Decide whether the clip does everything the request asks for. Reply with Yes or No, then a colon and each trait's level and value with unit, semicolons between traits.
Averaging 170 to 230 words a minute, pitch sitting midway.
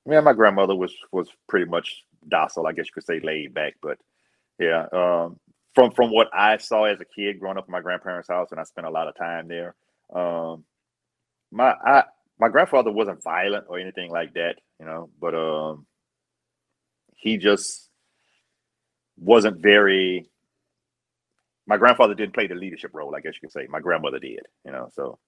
No: average, 185 wpm; very low, 90 Hz